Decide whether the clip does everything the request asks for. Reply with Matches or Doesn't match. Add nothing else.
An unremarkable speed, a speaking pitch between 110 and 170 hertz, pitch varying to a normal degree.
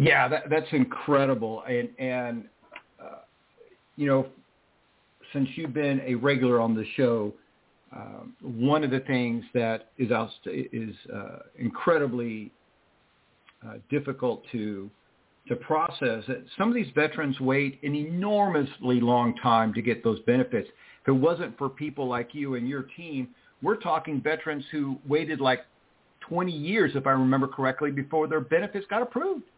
Matches